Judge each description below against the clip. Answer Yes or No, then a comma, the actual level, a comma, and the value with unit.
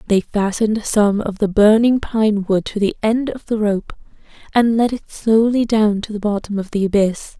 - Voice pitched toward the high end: Yes, high, 210 Hz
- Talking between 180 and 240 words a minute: Yes, fast, 205 wpm